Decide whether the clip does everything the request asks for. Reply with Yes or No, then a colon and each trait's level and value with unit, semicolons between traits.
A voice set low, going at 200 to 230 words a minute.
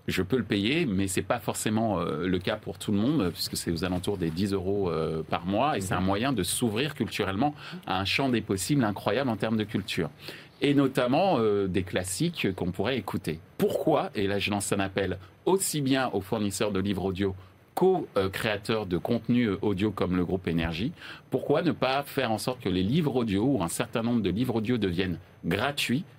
Yes: low, 105 Hz; average, 210 wpm